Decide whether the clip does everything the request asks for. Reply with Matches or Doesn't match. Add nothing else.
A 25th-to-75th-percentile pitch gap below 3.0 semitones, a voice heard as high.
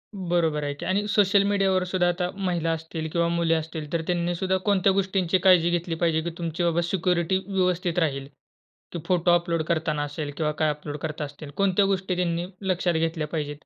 Doesn't match